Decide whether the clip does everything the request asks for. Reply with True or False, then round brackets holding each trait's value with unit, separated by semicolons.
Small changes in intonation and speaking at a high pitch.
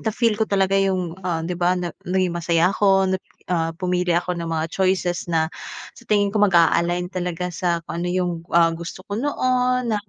False (2.2 semitones; 180 Hz)